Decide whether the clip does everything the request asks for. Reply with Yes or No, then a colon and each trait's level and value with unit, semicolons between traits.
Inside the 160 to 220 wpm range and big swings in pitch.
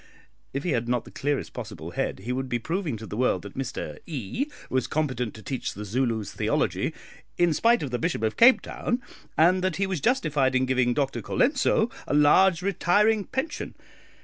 Yes: average, 195 wpm; wide, 7.2 semitones